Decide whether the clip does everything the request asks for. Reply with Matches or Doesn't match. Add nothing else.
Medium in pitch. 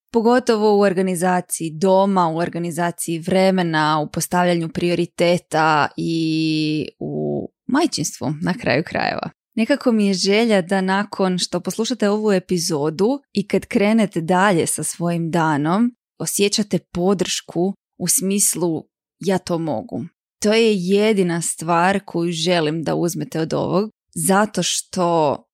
Matches